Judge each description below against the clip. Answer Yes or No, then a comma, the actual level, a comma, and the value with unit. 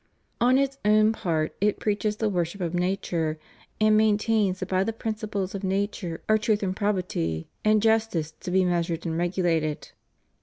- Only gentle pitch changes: No, average, 3.7 semitones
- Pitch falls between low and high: No, high, 195 Hz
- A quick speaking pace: No, average, 175 wpm